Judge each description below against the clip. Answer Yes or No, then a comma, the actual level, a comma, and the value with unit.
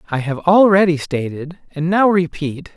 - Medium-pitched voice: Yes, medium, 165 Hz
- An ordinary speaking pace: Yes, average, 150 wpm